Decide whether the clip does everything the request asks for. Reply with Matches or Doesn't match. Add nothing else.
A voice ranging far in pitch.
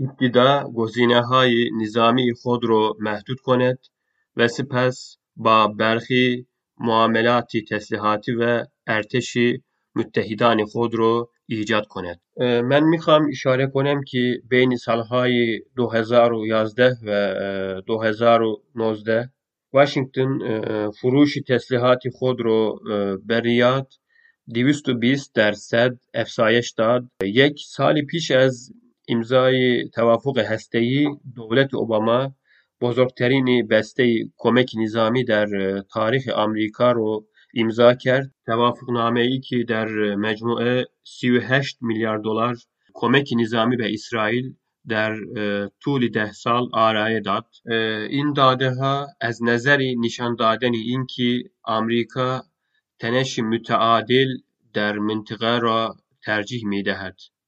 Doesn't match